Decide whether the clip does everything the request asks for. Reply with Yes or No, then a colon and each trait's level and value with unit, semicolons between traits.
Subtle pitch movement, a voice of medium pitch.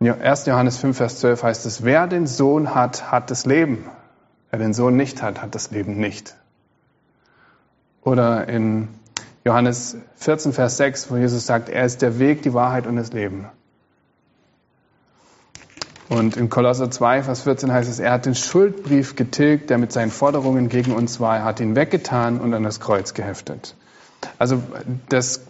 No: narrow, 2.1 semitones; low, 125 Hz